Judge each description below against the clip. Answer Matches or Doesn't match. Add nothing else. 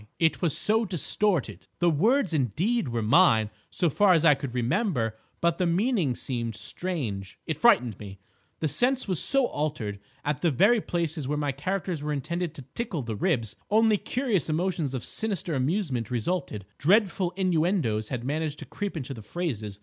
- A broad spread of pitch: Matches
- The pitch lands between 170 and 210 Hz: Doesn't match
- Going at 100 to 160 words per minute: Doesn't match